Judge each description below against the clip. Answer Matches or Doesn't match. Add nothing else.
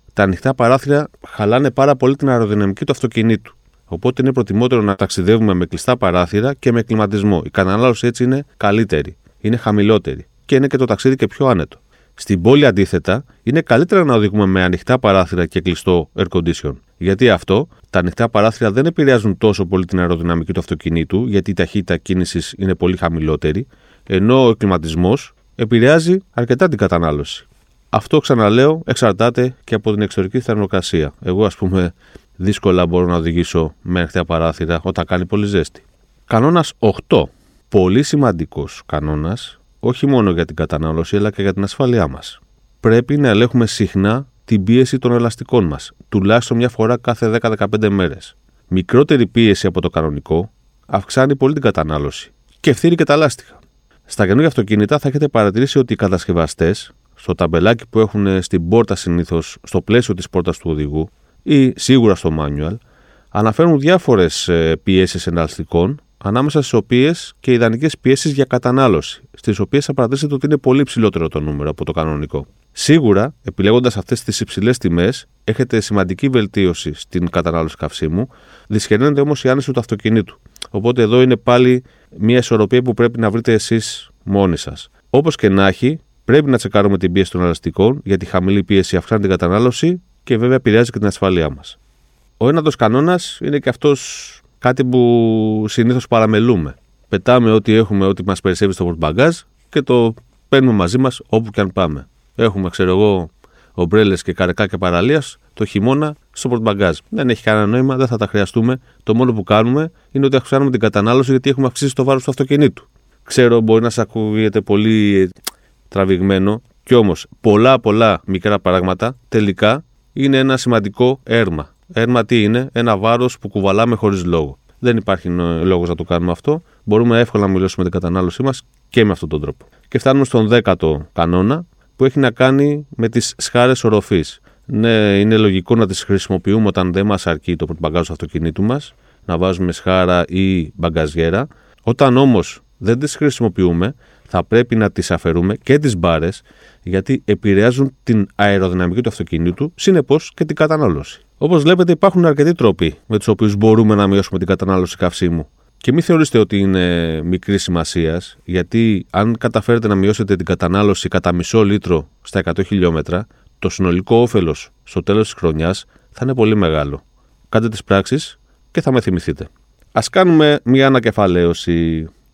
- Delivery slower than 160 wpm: Doesn't match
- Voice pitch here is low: Matches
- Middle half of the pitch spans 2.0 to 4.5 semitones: Doesn't match